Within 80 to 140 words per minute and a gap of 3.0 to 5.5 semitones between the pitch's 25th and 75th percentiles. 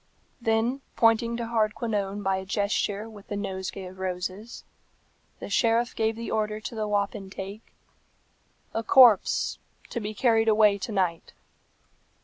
No: slow, 135 wpm; narrow, 2.4 semitones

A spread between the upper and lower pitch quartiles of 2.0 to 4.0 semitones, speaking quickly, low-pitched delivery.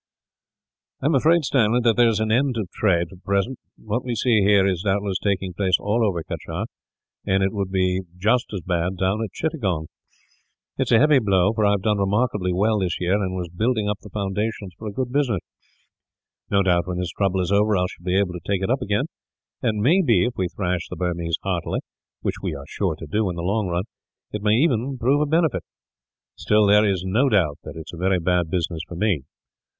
Yes: average, 3.6 semitones; fast, 230 wpm; low, 100 Hz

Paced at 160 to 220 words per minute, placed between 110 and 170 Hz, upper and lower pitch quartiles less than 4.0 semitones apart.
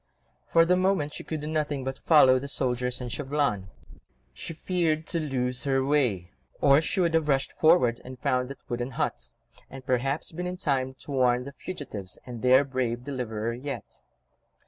Yes: average, 180 wpm; low, 135 Hz; average, 3.3 semitones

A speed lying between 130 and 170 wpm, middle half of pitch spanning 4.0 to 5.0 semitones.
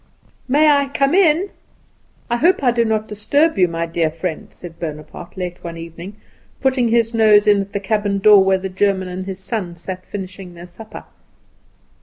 No: average, 185 wpm; average, 4.5 semitones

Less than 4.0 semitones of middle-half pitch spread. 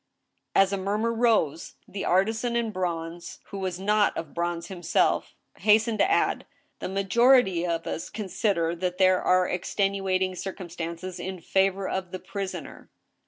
Yes: average, 2.7 semitones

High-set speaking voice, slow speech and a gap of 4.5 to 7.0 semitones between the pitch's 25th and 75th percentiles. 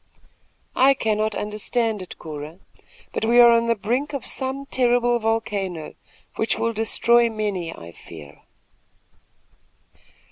No: high, 225 Hz; slow, 120 wpm; average, 3.3 semitones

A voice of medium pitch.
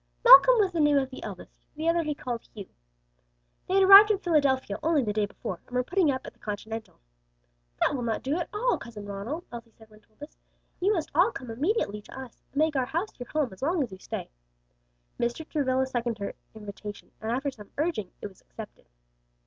No: very high, 265 Hz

